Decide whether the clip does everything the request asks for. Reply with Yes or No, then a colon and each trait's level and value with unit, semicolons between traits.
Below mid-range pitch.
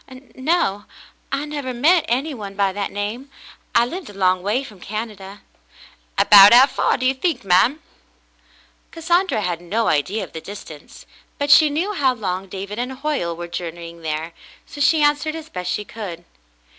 No: high, 220 Hz